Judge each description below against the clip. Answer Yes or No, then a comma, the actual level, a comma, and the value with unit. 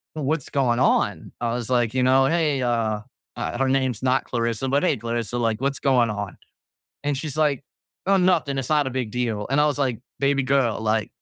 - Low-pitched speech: Yes, low, 130 Hz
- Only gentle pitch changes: No, average, 3.1 semitones